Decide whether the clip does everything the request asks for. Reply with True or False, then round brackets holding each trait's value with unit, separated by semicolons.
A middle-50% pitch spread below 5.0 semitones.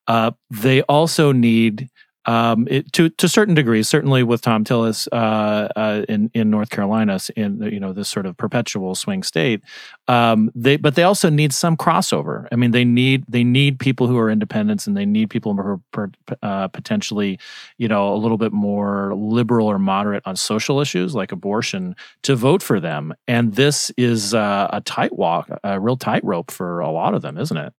False (5.4 semitones)